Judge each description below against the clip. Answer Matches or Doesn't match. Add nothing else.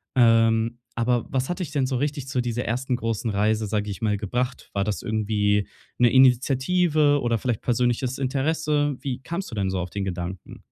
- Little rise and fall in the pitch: Doesn't match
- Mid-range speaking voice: Doesn't match